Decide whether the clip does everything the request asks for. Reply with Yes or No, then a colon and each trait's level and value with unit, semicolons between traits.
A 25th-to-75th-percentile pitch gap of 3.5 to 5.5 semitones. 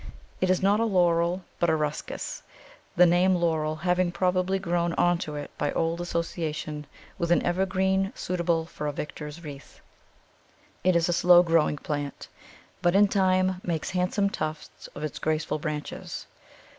No: average, 2.9 semitones